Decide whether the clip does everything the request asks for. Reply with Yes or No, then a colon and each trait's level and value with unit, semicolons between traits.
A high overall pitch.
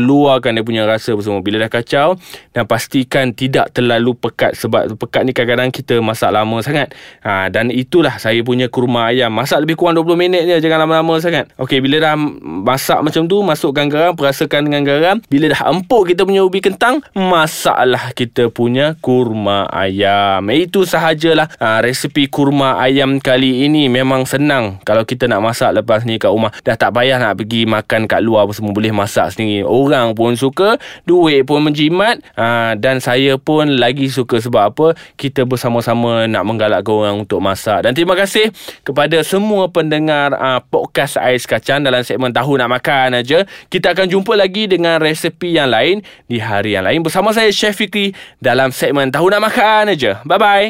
No: low, 135 Hz